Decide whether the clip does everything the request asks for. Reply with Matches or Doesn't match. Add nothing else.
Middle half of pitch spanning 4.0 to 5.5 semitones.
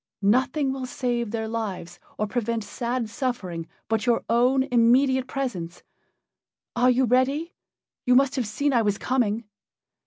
Doesn't match